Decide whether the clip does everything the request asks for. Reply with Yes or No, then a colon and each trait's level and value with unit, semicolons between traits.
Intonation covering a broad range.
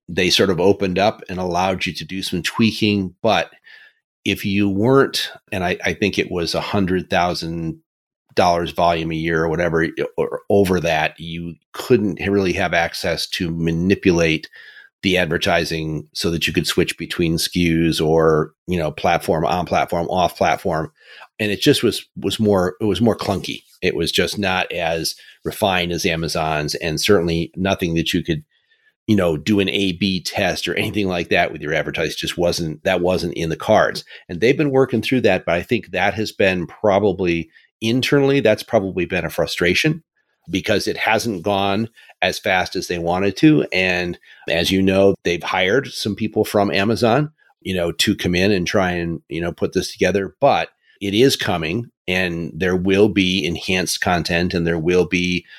No: average, 3.6 semitones